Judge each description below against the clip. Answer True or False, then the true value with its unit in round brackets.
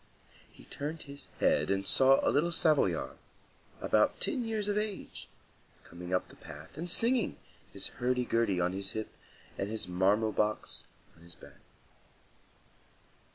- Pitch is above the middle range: False (115 Hz)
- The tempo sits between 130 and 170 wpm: True (150 wpm)